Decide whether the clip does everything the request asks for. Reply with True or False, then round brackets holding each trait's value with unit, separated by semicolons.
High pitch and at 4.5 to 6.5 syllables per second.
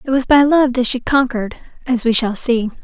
True (250 Hz; 5.5 syllables/s)